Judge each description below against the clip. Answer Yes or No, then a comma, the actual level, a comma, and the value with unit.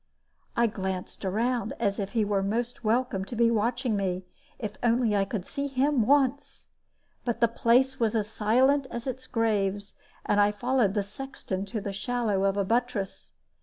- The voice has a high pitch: Yes, high, 225 Hz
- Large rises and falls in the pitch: No, average, 3.6 semitones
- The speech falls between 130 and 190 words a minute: Yes, average, 175 wpm